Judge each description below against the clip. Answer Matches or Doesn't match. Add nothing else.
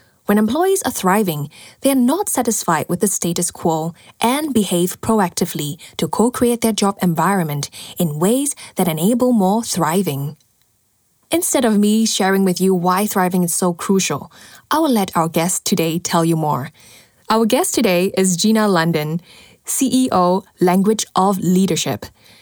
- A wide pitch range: Doesn't match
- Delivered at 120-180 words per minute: Matches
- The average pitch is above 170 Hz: Matches